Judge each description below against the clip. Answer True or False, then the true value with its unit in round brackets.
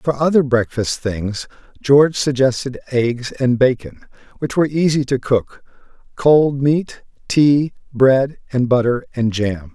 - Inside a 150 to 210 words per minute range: False (135 wpm)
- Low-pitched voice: True (130 Hz)